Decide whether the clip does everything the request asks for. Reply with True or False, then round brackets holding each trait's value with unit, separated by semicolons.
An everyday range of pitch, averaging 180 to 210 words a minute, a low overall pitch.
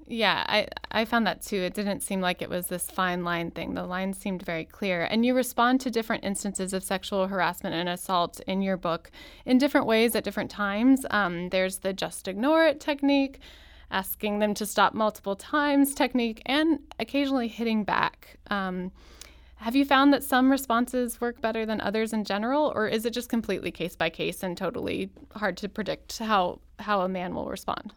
False (4.8 semitones; 195 wpm; 210 Hz)